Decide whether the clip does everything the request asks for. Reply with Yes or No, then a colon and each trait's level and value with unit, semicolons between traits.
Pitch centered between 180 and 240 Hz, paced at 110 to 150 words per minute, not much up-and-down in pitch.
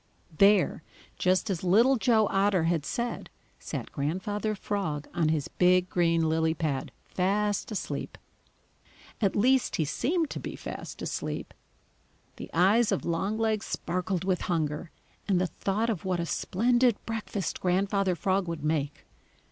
No: medium, 185 Hz; average, 140 wpm; average, 3.9 semitones